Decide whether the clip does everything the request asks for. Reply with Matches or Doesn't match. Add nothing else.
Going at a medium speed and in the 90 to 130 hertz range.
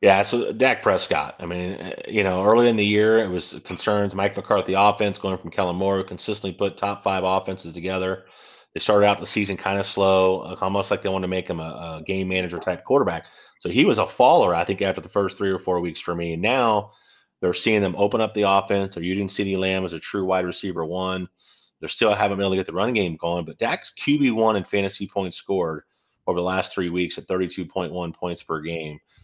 Doesn't match